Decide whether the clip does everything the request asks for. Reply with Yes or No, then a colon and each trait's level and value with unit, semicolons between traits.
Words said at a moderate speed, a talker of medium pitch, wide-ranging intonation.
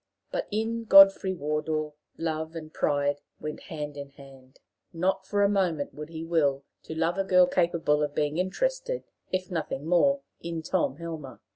No: average, 165 wpm; medium, 165 Hz; average, 4.0 semitones